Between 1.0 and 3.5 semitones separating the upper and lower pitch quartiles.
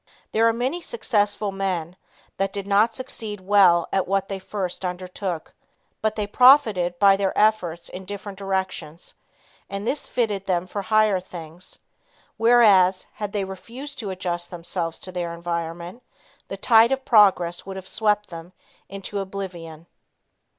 Yes: average, 2.9 semitones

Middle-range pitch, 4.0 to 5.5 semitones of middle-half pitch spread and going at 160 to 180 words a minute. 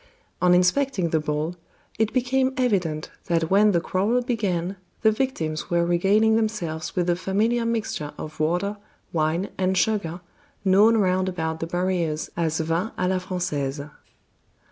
No: medium, 180 Hz; average, 4.5 semitones; average, 145 wpm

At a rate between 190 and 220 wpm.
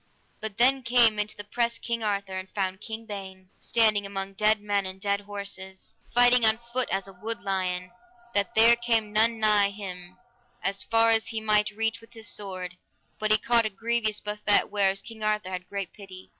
Yes: average, 195 wpm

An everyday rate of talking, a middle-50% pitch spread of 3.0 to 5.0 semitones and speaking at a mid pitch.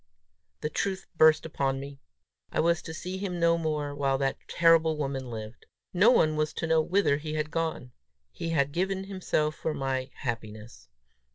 Yes: average, 175 wpm; average, 3.6 semitones; medium, 155 Hz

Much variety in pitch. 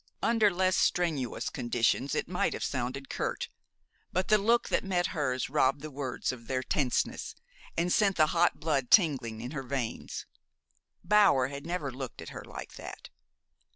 Yes: wide, 5.7 semitones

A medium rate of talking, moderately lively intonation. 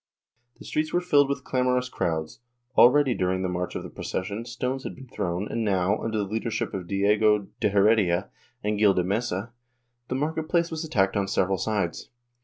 Yes: average, 190 wpm; average, 4.7 semitones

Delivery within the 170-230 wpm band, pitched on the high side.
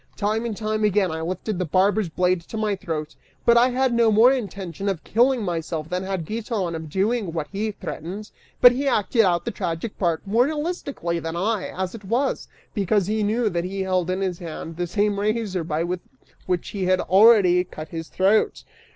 Yes: average, 200 wpm; high, 195 Hz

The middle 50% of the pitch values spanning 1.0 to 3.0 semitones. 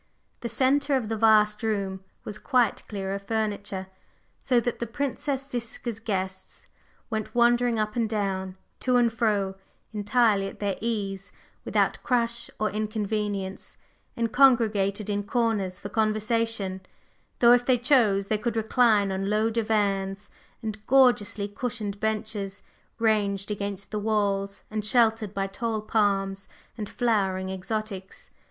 Yes: average, 2.7 semitones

